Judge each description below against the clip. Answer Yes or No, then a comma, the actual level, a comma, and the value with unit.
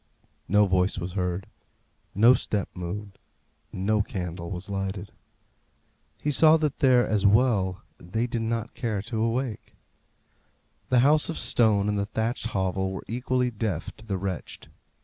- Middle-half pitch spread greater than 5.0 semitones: No, average, 3.9 semitones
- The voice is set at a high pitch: No, low, 105 Hz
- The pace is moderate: Yes, average, 150 wpm